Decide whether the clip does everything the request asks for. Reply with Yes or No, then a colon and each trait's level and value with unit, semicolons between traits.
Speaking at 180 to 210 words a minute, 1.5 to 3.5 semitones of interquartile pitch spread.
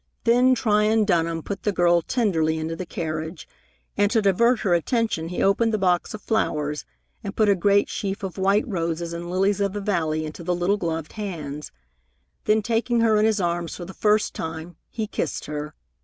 No: average, 195 wpm; average, 4.3 semitones